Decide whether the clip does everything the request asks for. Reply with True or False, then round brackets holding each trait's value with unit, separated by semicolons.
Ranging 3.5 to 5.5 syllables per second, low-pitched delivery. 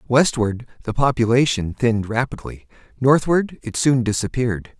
True (4.9 syllables/s; 120 Hz)